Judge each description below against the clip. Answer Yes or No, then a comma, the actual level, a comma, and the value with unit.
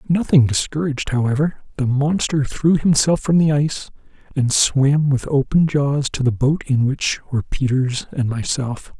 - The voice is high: No, medium, 140 Hz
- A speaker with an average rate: Yes, average, 160 wpm